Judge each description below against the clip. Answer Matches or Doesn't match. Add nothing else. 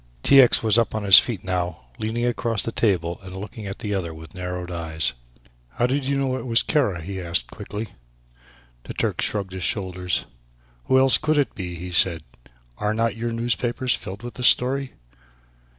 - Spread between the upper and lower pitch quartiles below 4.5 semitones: Doesn't match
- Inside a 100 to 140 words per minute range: Doesn't match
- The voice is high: Doesn't match